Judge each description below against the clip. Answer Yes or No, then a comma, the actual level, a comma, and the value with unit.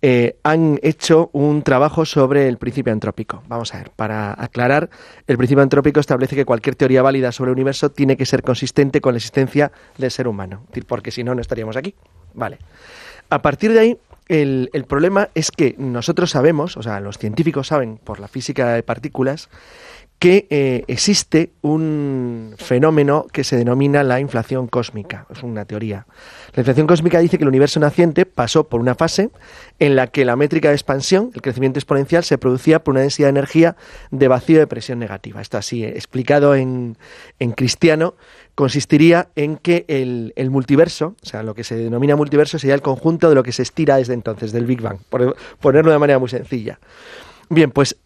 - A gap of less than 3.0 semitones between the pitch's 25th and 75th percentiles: No, average, 3.9 semitones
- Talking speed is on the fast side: No, average, 190 wpm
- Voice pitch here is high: No, low, 135 Hz